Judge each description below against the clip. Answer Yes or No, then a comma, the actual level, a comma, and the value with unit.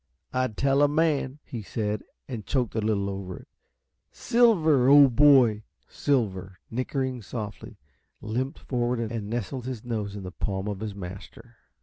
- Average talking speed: Yes, average, 150 wpm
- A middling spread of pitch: Yes, average, 4.3 semitones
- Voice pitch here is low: Yes, low, 115 Hz